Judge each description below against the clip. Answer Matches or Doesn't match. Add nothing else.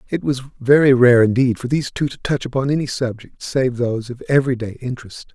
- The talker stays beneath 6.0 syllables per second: Doesn't match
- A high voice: Doesn't match